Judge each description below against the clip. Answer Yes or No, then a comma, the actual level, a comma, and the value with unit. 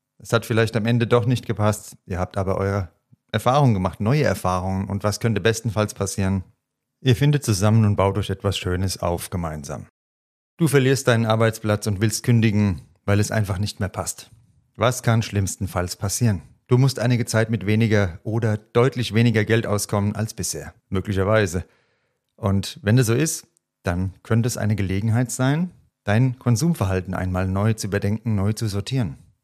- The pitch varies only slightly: No, average, 3.4 semitones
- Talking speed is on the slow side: No, average, 165 wpm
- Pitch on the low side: Yes, low, 110 Hz